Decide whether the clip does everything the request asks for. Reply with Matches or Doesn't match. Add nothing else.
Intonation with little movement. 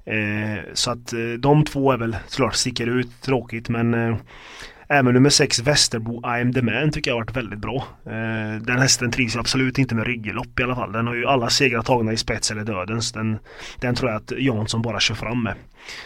Matches